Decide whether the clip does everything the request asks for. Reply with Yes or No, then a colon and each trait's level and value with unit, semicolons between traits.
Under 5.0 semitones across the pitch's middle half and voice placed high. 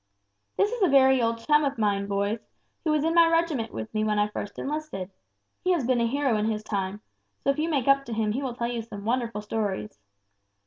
No: average, 5.3 semitones; high, 235 Hz